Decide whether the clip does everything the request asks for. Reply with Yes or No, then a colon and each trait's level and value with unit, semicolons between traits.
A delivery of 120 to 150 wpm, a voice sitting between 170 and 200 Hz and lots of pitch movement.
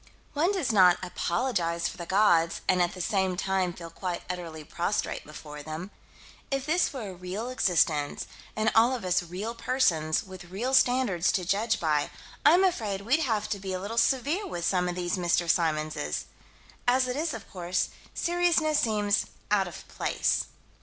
No: average, 175 wpm; high, 190 Hz; wide, 6.0 semitones